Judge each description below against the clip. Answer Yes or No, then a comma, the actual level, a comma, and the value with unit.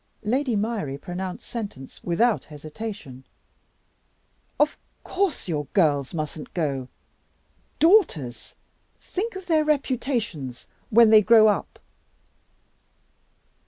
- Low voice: No, high, 210 Hz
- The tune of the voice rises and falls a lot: Yes, wide, 9.0 semitones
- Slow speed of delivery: Yes, slow, 90 wpm